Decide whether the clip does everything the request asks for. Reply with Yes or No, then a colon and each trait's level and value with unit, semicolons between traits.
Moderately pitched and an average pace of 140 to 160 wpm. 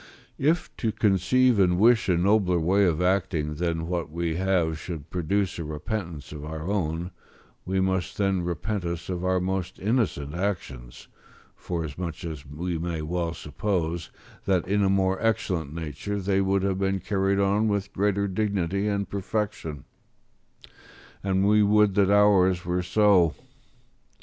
No: very low, 95 Hz; average, 150 wpm